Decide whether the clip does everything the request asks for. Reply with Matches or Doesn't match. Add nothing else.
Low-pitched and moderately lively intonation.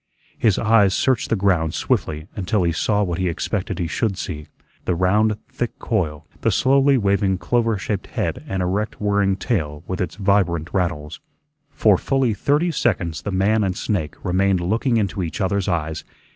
Matches